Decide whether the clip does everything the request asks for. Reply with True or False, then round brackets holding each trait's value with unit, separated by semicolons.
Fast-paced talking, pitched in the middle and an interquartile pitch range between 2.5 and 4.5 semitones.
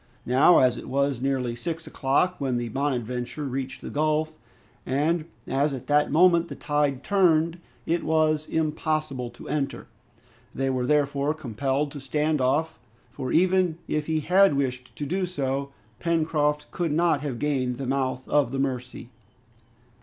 False (155 wpm; 145 Hz; 3.0 semitones)